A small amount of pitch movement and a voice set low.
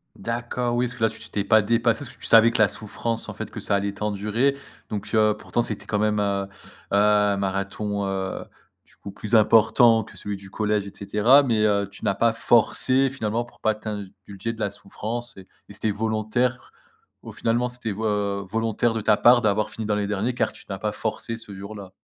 Yes: narrow, 2.3 semitones; low, 105 Hz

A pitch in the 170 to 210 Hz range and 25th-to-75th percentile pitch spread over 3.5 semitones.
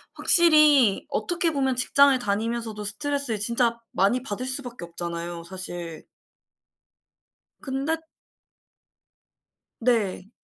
No: high, 235 Hz; wide, 5.5 semitones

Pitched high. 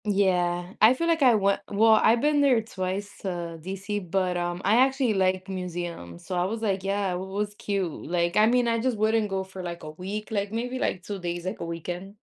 Yes: high, 195 Hz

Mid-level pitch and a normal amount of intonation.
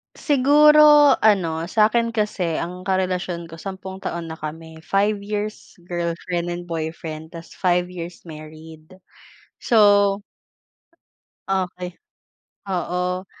Yes: medium, 180 Hz; average, 3.4 semitones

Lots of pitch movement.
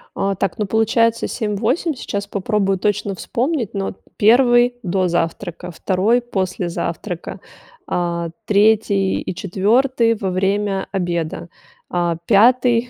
No: average, 3.7 semitones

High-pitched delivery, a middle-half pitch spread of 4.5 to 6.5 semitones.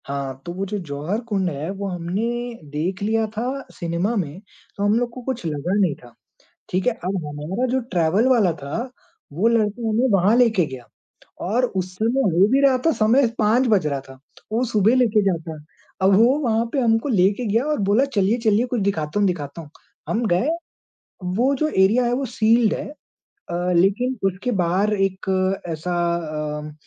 Yes: high, 200 Hz; average, 5.2 semitones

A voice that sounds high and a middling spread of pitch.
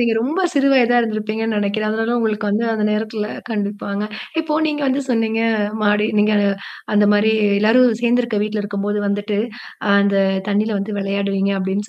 No: high, 215 Hz; narrow, 1.8 semitones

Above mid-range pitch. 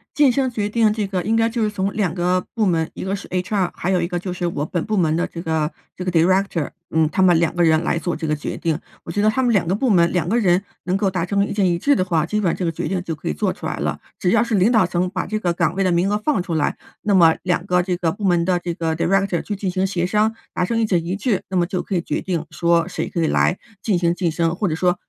No: medium, 180 Hz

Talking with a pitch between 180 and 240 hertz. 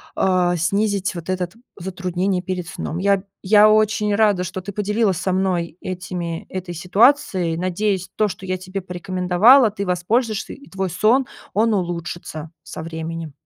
Yes: medium, 185 Hz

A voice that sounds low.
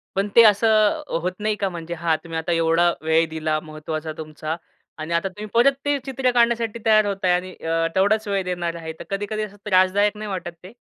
No: medium, 185 Hz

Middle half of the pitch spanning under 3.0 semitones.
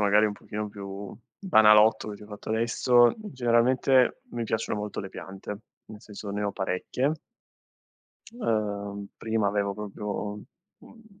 Yes: narrow, 2.5 semitones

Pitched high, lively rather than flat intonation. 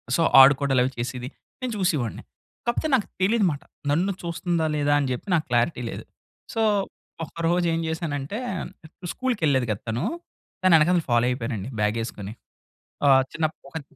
No: medium, 150 Hz; wide, 5.7 semitones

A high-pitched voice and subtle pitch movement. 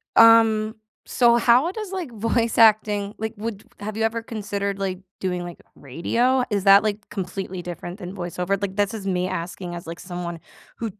No: high, 205 Hz; average, 3.7 semitones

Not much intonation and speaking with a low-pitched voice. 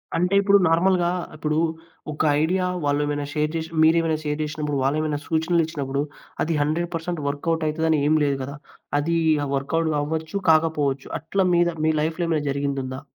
No: narrow, 2.3 semitones; medium, 155 Hz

